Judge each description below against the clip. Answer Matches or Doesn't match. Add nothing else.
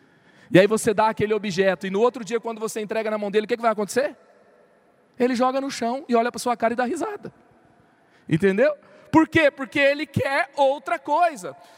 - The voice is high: Matches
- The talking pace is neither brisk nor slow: Doesn't match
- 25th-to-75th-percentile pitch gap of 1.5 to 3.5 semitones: Doesn't match